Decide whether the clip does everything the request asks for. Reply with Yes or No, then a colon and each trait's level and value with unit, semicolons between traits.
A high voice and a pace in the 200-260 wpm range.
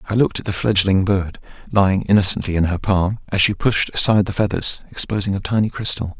No: low, 100 Hz; fast, 205 wpm